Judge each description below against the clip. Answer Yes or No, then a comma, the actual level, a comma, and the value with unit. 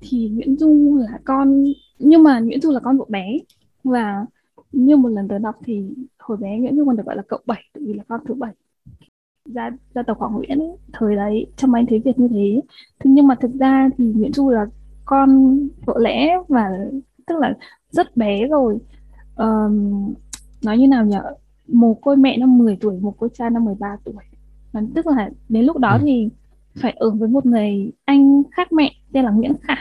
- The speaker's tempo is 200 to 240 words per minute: Yes, average, 205 wpm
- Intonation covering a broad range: No, average, 3.9 semitones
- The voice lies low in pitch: No, very high, 250 Hz